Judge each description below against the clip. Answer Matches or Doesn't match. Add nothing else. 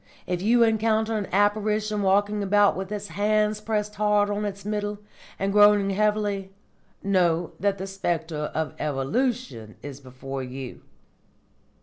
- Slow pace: Matches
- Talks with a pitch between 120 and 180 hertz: Doesn't match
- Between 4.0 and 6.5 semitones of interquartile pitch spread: Doesn't match